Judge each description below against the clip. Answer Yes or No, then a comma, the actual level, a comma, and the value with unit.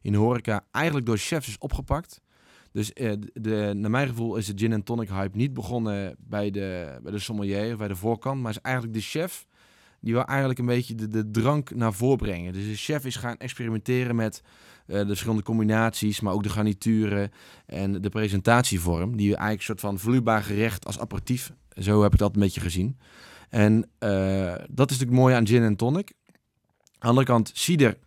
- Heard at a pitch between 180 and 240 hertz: No, low, 110 Hz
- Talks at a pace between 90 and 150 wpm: No, average, 190 wpm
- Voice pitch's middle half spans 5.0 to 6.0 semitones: No, average, 2.9 semitones